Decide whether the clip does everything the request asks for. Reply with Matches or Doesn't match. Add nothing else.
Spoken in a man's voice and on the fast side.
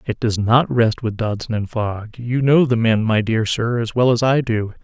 Matches